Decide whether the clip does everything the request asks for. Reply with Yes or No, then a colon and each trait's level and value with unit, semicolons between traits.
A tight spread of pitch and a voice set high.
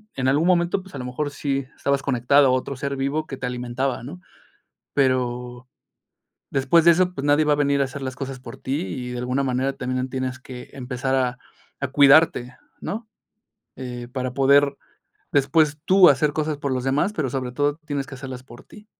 No: narrow, 2.2 semitones; low, 135 Hz